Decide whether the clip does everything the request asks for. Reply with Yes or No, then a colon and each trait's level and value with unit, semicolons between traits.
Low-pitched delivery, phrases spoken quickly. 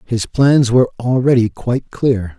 No: low, 120 Hz; average, 150 wpm